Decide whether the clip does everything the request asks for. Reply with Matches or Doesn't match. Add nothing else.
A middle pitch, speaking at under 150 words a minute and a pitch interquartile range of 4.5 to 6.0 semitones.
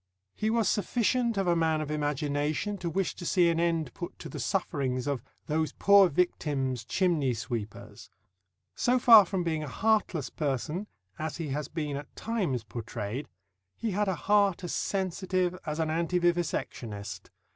Doesn't match